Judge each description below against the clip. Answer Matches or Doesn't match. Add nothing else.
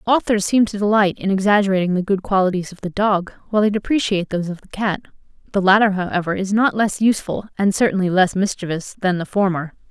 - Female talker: Matches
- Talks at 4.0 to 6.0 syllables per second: Doesn't match